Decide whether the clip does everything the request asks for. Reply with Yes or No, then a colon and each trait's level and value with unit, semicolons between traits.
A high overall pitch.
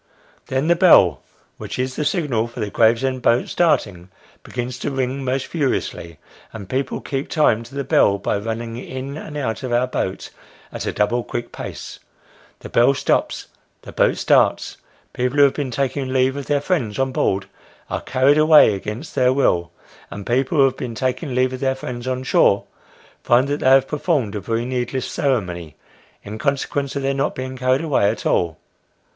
No: low, 130 Hz